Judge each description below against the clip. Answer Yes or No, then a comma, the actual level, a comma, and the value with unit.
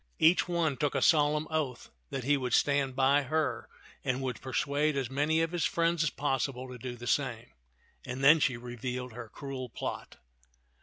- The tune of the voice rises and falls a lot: No, average, 3.1 semitones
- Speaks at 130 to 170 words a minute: No, average, 185 wpm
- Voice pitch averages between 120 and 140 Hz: Yes, low, 135 Hz